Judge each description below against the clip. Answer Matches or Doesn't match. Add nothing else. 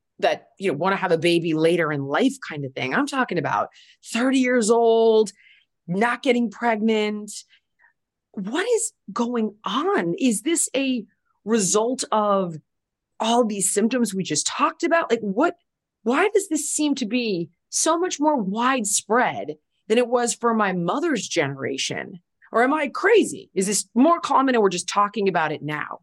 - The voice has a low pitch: Doesn't match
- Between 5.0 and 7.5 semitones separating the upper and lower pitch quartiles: Matches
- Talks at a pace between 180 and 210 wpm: Doesn't match